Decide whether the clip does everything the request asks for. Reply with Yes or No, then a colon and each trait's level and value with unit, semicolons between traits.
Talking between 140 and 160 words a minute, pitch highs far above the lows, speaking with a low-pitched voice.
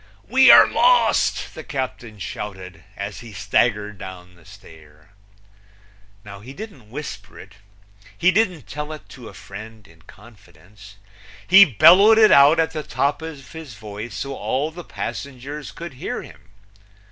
Yes: average, 145 wpm; wide, 7.2 semitones; low, 125 Hz